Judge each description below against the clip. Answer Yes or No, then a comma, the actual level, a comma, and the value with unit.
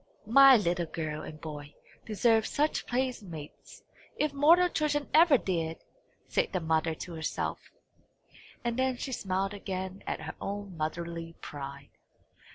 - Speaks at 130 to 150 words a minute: Yes, slow, 135 wpm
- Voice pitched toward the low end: No, high, 190 Hz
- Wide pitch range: Yes, wide, 8.1 semitones